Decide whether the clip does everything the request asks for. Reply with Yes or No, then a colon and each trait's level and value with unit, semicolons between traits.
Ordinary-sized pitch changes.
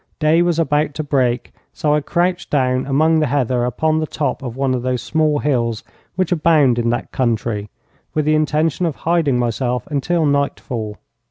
Yes: average, 4.0 semitones